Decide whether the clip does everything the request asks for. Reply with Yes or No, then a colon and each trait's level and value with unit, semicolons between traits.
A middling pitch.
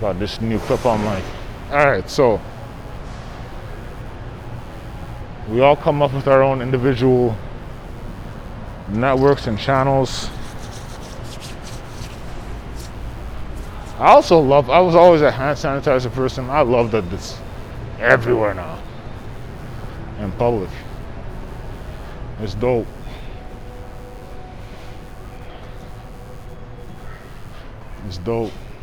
No: low, 125 Hz